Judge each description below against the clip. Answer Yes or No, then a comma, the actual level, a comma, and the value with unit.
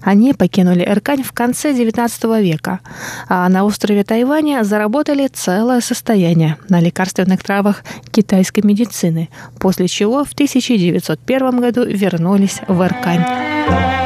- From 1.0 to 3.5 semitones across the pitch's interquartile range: No, average, 4.7 semitones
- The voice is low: No, high, 205 Hz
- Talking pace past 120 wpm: No, average, 115 wpm